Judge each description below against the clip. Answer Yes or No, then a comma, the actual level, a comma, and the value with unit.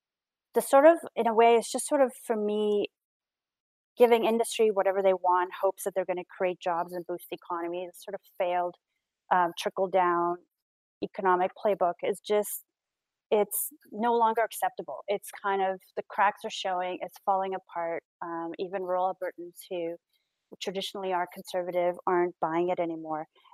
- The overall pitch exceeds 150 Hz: Yes, high, 190 Hz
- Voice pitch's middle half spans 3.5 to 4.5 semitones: No, average, 2.9 semitones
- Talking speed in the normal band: Yes, average, 165 wpm